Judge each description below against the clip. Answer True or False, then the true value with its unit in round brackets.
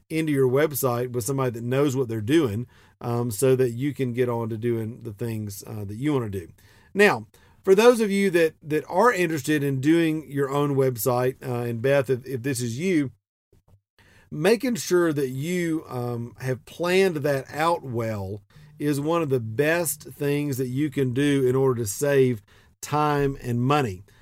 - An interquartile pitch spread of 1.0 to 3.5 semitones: False (4.0 semitones)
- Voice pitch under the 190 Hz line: True (135 Hz)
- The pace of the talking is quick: False (190 wpm)